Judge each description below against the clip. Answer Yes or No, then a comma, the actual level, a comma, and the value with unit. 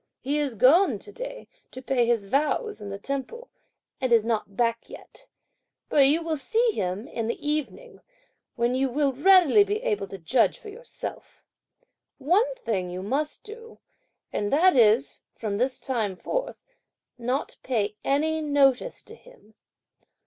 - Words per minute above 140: Yes, average, 160 wpm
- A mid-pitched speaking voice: No, very high, 275 Hz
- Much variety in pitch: Yes, wide, 8.7 semitones